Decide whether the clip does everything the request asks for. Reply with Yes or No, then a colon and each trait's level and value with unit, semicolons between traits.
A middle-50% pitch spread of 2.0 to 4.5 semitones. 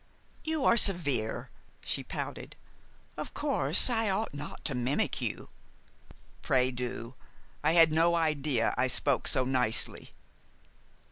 No: average, 5.2 semitones